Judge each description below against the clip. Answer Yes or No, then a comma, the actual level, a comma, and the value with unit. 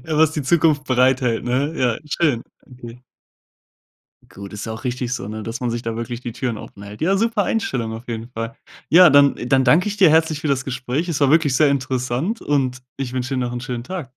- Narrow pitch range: No, average, 4.0 semitones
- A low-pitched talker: Yes, low, 130 Hz